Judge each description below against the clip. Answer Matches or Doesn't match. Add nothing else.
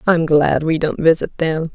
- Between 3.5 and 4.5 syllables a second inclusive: Matches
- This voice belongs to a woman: Matches